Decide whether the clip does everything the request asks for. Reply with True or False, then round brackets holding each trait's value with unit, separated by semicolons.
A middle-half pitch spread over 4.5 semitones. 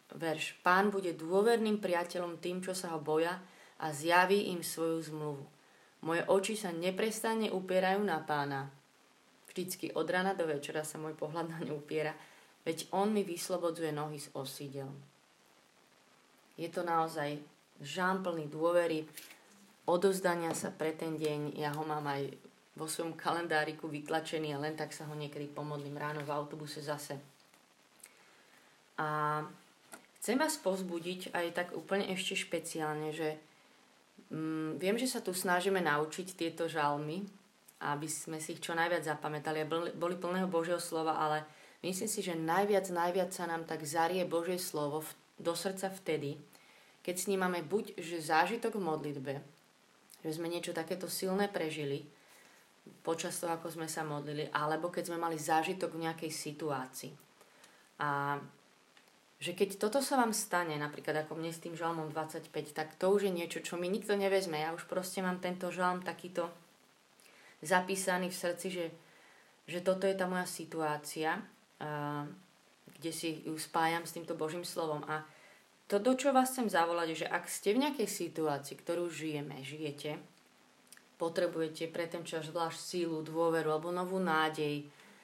False (2.9 semitones)